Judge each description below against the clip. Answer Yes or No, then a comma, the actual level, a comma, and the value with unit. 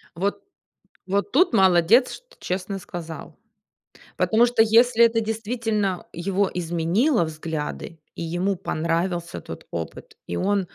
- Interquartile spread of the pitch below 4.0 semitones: No, average, 4.7 semitones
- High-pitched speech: Yes, high, 195 Hz